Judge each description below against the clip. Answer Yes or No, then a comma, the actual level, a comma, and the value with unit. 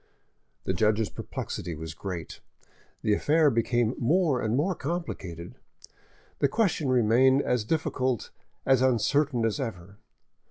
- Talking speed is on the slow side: Yes, slow, 120 wpm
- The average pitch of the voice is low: Yes, low, 125 Hz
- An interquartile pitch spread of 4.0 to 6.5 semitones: Yes, average, 5.1 semitones